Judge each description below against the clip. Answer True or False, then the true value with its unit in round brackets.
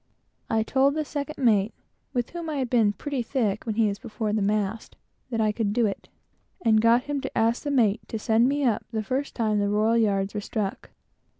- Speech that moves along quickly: True (210 wpm)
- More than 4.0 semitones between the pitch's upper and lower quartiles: False (3.6 semitones)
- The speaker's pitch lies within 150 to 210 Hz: False (225 Hz)